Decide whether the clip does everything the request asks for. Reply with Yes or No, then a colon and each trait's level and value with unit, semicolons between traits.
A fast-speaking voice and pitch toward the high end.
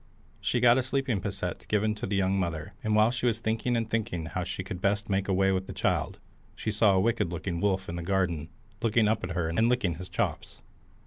No: fast, 235 wpm; low, 100 Hz